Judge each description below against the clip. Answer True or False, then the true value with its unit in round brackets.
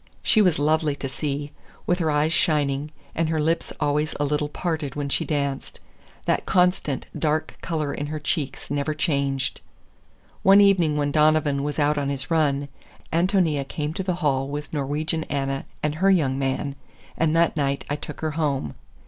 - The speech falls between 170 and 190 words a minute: True (175 wpm)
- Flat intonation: True (2.2 semitones)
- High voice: False (150 Hz)